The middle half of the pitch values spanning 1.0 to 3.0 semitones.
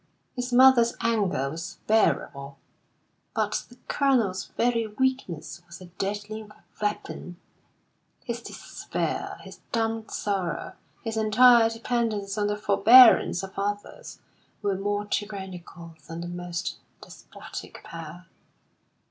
No: average, 4.2 semitones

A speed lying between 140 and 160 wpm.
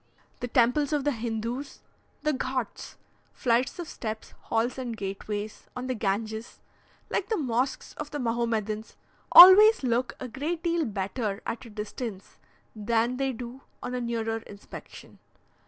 Yes: average, 145 wpm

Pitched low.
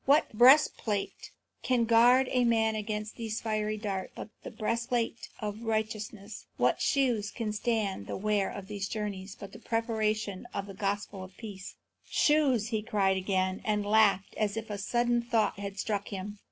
No: high, 215 Hz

